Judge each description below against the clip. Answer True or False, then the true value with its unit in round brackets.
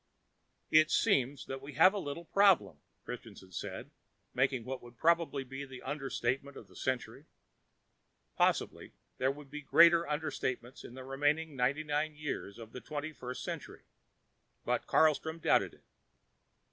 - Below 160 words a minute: True (145 wpm)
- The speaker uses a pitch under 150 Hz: True (140 Hz)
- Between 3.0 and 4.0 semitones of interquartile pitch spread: True (3.4 semitones)